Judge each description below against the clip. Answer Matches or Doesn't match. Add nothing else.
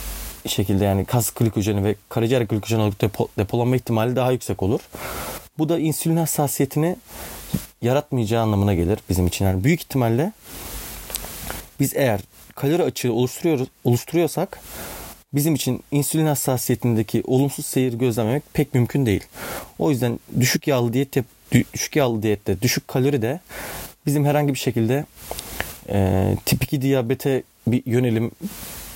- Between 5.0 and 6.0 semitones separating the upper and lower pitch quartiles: Doesn't match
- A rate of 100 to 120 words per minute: Doesn't match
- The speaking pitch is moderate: Doesn't match